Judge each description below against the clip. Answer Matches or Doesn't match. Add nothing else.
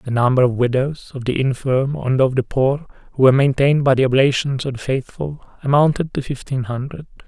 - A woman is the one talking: Doesn't match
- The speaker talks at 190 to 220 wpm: Matches